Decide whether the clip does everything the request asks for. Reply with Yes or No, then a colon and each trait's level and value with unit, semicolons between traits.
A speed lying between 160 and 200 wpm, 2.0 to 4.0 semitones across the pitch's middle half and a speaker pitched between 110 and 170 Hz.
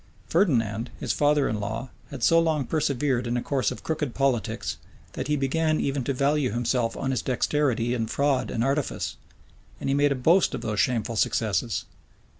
Yes: average, 185 wpm; average, 3.7 semitones; low, 135 Hz